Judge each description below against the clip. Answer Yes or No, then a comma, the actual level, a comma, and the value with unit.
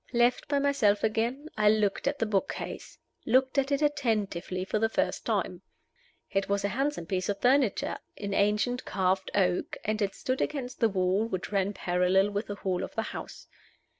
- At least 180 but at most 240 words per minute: Yes, average, 190 wpm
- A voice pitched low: No, high, 210 Hz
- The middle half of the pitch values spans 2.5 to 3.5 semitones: No, average, 4.4 semitones